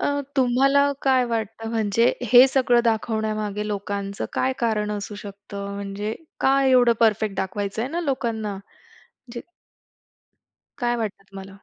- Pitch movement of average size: Yes, average, 3.2 semitones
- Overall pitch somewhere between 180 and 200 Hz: No, high, 220 Hz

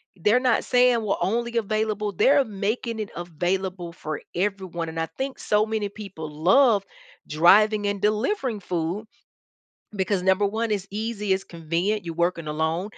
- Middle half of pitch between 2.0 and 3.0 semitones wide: No, average, 3.8 semitones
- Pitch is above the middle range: Yes, high, 200 Hz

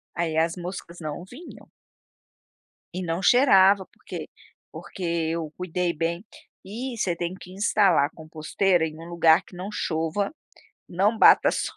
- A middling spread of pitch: Yes, average, 3.0 semitones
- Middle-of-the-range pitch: Yes, medium, 180 Hz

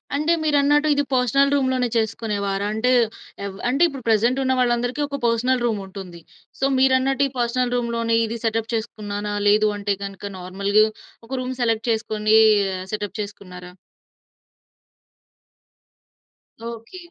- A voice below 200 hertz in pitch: No, high, 230 Hz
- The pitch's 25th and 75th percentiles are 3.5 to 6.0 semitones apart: Yes, average, 3.8 semitones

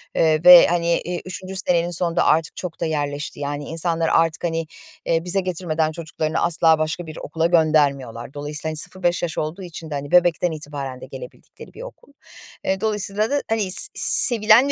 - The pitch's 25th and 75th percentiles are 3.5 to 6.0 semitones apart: No, narrow, 2.5 semitones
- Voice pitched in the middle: Yes, medium, 165 Hz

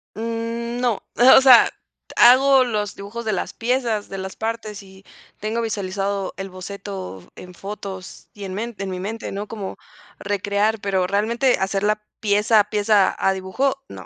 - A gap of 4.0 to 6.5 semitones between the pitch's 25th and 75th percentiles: No, average, 2.8 semitones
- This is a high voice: Yes, high, 205 Hz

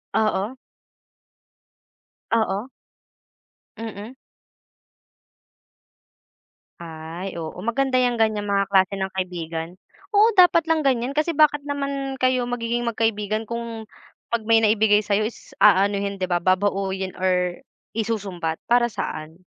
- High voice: Yes, high, 215 Hz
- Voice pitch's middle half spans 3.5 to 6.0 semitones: Yes, average, 4.2 semitones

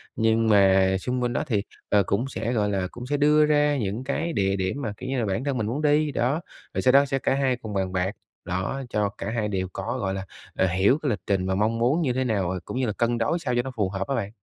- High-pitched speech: No, low, 115 Hz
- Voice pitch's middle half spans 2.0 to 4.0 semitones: No, average, 5.3 semitones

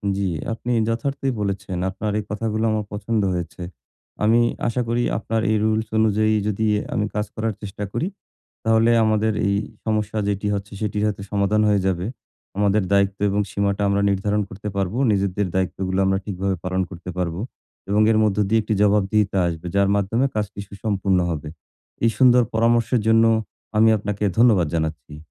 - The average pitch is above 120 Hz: No, low, 105 Hz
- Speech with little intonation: Yes, narrow, 2.1 semitones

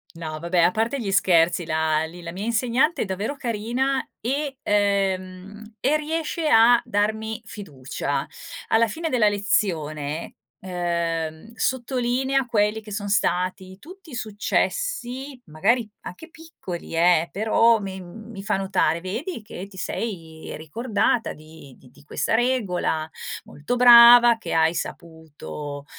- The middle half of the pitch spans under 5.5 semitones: No, wide, 6.0 semitones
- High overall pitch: Yes, high, 205 Hz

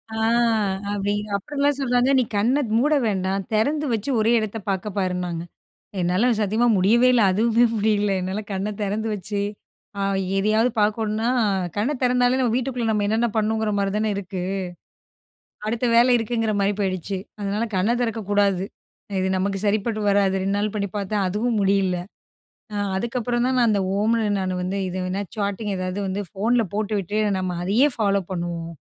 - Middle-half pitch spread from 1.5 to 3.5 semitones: Yes, average, 2.8 semitones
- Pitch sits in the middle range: No, high, 210 Hz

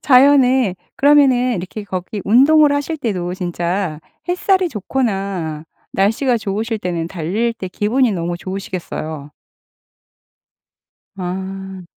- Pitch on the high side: Yes, high, 200 Hz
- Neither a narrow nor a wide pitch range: No, wide, 5.9 semitones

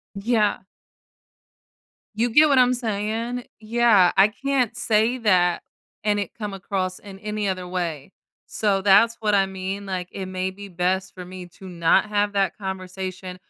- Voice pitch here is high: Yes, high, 200 Hz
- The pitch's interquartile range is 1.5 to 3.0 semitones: Yes, average, 2.7 semitones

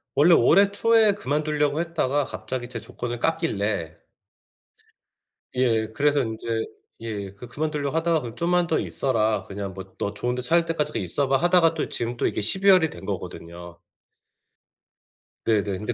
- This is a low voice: Yes, low, 130 Hz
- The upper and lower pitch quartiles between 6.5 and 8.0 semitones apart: Yes, wide, 6.9 semitones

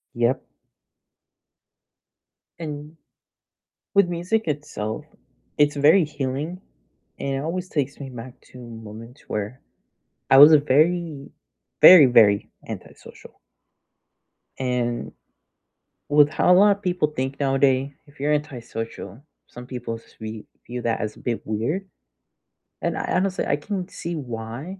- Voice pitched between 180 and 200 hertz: No, medium, 140 Hz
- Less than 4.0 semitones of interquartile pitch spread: No, average, 4.9 semitones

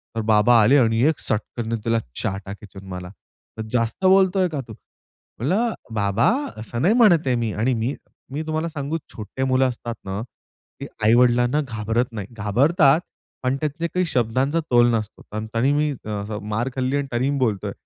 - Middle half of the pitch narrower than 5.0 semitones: Yes, average, 4.5 semitones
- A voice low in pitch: Yes, low, 120 Hz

